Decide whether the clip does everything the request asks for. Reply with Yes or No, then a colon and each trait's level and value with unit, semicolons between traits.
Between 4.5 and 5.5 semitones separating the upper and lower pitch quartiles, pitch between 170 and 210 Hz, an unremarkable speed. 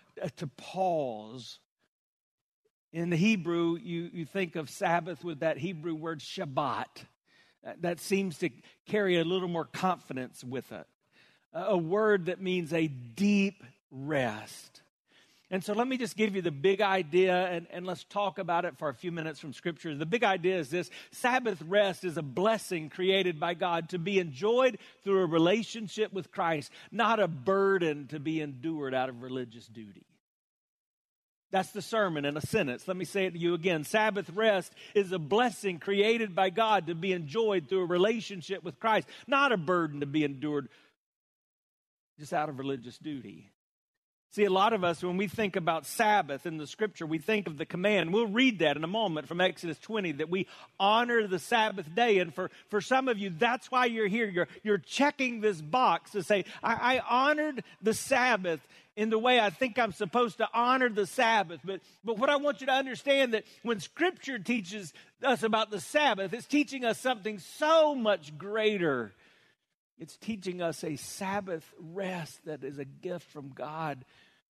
Yes: average, 4.8 semitones; medium, 185 Hz; average, 180 wpm